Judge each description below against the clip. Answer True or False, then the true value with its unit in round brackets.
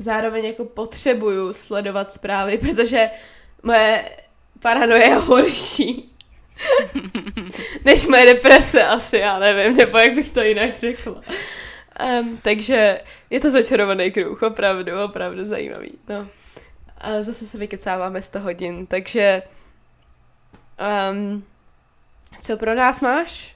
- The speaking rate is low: True (110 wpm)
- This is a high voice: True (220 Hz)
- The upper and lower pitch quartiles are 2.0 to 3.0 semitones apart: False (3.5 semitones)